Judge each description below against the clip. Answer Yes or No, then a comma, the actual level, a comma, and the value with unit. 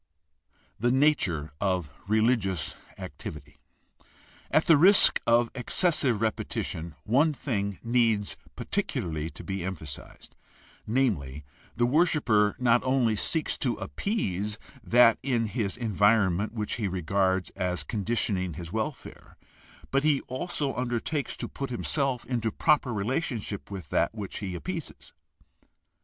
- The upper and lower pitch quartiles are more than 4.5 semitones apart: Yes, average, 5.1 semitones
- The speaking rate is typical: No, slow, 125 wpm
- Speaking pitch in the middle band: No, low, 110 Hz